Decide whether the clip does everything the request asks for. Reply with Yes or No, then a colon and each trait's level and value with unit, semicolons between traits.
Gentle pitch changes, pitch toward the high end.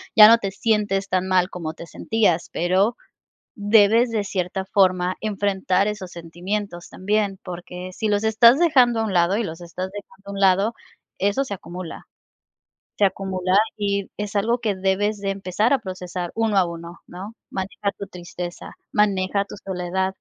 Yes: narrow, 2.3 semitones; high, 195 Hz